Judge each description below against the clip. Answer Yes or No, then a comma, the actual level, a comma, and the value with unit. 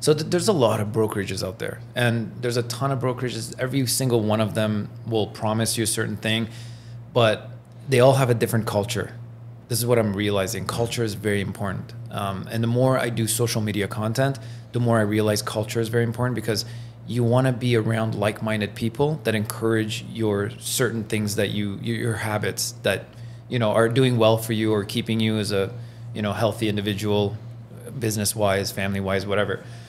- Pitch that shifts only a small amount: Yes, narrow, 1.9 semitones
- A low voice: Yes, low, 115 Hz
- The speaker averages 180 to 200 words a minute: Yes, average, 195 wpm